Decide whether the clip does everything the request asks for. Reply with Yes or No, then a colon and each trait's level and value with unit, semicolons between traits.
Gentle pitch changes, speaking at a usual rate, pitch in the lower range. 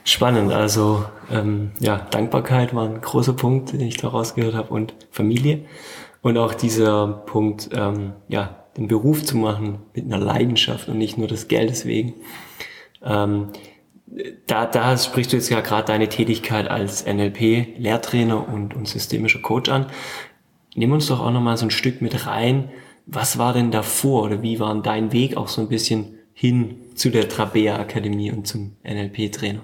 Yes: narrow, 2.3 semitones; average, 170 wpm; low, 110 Hz